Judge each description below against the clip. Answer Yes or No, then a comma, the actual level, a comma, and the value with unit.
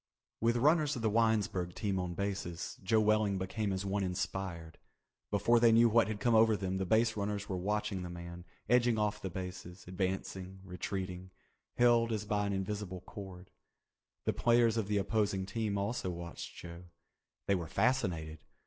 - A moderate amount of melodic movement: Yes, average, 3.1 semitones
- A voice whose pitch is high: No, low, 100 Hz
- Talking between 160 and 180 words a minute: Yes, average, 170 wpm